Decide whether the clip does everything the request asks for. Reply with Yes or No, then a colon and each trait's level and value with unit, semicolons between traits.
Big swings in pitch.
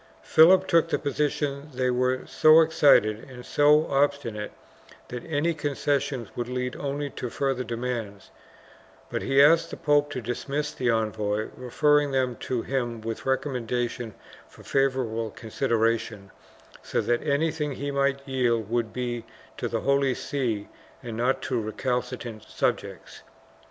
No: average, 3.4 semitones